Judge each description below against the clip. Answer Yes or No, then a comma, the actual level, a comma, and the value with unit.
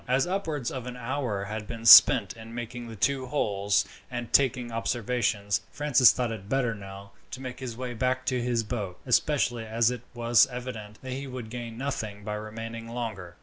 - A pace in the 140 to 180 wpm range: No, average, 190 wpm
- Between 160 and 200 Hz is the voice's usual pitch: No, low, 120 Hz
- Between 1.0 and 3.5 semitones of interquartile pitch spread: Yes, average, 2.7 semitones